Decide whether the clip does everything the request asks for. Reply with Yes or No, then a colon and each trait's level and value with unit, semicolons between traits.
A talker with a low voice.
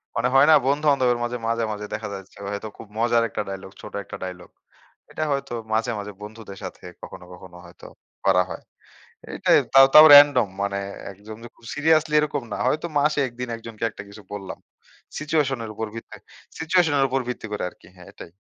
Yes: low, 115 Hz